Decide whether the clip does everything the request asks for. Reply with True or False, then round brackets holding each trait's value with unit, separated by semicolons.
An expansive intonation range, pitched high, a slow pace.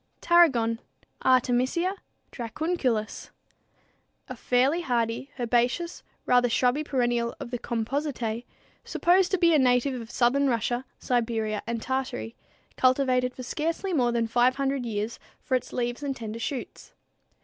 False (2.9 semitones; 250 Hz; 130 wpm)